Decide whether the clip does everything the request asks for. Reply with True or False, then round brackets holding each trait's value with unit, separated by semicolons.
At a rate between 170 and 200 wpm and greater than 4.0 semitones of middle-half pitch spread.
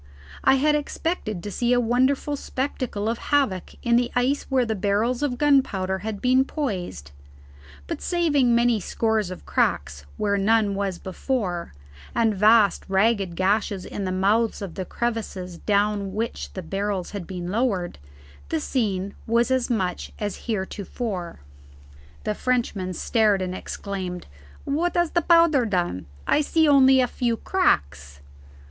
False (145 wpm; 5.0 semitones)